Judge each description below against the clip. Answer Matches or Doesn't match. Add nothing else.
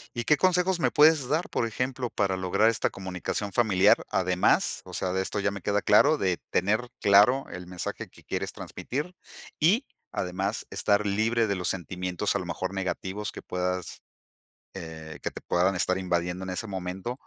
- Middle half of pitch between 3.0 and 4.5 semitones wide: Matches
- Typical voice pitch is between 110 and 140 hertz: Doesn't match